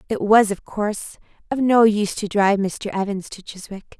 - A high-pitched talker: Yes, high, 205 Hz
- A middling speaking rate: Yes, average, 195 wpm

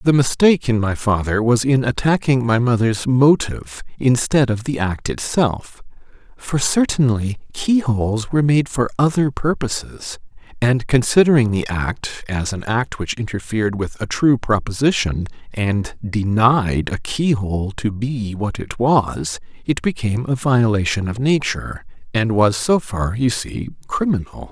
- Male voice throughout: Yes, male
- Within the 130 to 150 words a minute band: Yes, average, 145 wpm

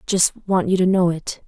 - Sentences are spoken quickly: Yes, fast, 285 wpm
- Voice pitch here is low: No, medium, 180 Hz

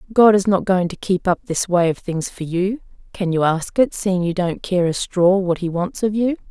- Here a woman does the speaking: Yes, female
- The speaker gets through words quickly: Yes, fast, 260 wpm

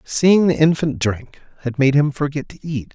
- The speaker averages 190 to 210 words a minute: Yes, fast, 205 wpm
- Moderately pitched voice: Yes, medium, 145 Hz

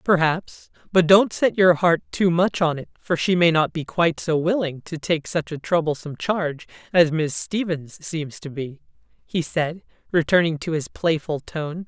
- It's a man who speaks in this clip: No, female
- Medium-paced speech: Yes, average, 185 wpm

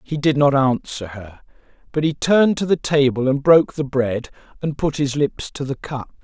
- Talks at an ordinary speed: No, fast, 210 wpm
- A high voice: No, medium, 140 Hz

